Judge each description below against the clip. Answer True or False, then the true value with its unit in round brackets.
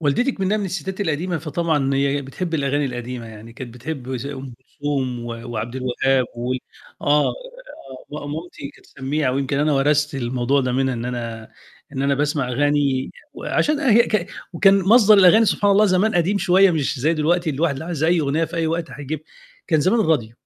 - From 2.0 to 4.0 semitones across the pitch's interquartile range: False (4.7 semitones)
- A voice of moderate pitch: True (145 Hz)